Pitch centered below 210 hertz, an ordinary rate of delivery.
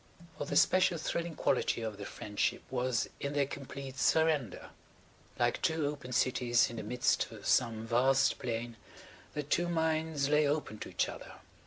Yes: low, 135 Hz; average, 165 wpm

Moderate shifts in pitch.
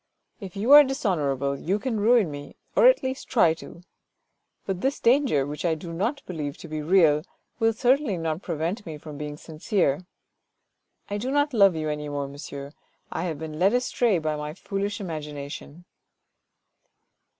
No: wide, 6.5 semitones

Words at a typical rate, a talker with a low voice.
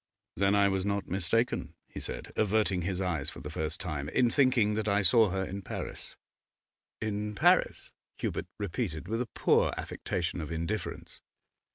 Yes: average, 165 wpm; low, 100 Hz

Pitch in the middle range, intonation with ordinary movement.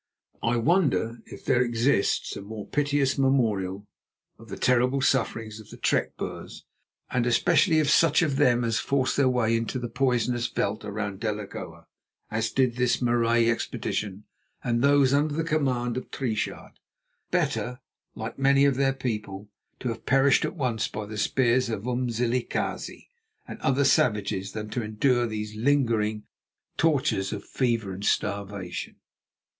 No: low, 120 Hz; average, 3.7 semitones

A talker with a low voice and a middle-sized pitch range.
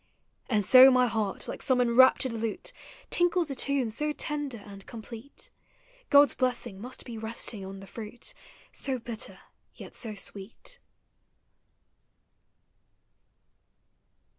No: high, 240 Hz; average, 3.7 semitones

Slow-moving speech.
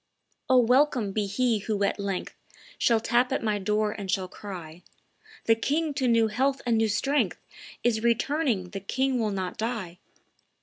No: average, 170 wpm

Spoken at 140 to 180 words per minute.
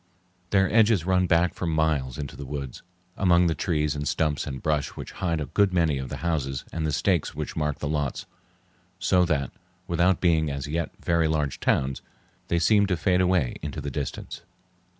No: average, 190 wpm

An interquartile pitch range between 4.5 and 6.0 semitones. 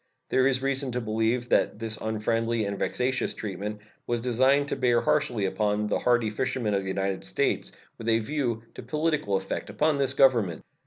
No: average, 3.7 semitones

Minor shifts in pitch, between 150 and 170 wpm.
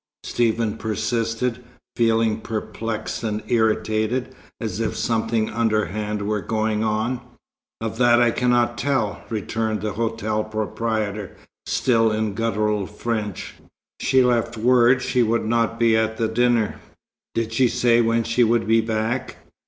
No: narrow, 1.5 semitones; slow, 135 wpm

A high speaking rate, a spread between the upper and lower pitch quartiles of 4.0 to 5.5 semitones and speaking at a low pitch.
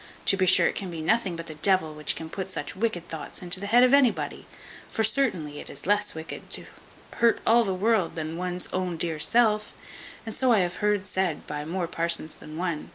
No: fast, 220 wpm; average, 4.4 semitones; medium, 185 Hz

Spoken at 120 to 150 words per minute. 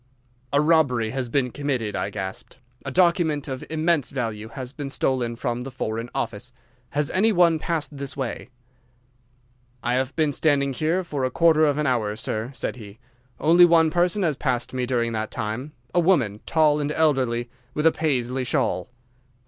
No: average, 170 wpm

